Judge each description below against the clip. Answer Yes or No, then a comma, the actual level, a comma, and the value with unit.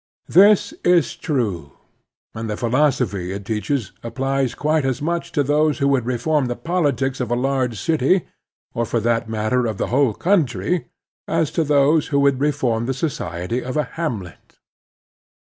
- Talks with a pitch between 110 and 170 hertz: Yes, low, 135 Hz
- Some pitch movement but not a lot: Yes, average, 4.5 semitones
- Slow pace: No, average, 165 wpm